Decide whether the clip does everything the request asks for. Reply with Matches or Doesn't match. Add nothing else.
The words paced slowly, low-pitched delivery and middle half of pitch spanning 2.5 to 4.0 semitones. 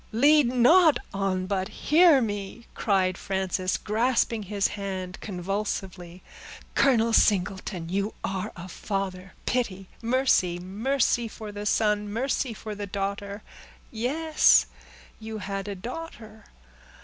Doesn't match